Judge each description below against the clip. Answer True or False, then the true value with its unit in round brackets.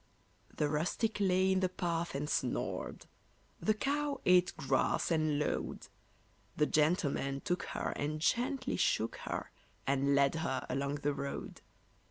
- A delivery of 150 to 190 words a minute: False (140 wpm)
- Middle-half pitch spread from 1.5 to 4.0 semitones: False (5.0 semitones)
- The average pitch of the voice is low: False (155 Hz)